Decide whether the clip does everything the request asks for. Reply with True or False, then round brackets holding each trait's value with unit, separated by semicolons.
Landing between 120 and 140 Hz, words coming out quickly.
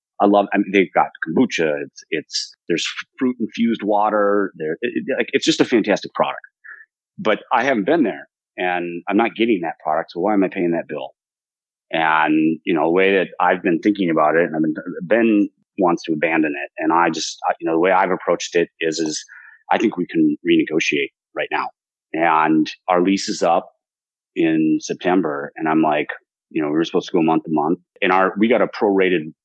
False (110 Hz; 210 wpm)